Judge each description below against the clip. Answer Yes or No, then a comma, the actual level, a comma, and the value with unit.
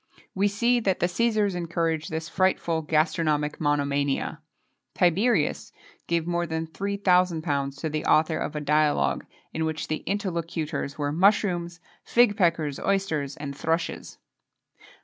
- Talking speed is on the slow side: Yes, slow, 130 wpm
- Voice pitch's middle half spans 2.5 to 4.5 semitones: Yes, average, 3.4 semitones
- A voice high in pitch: No, medium, 165 Hz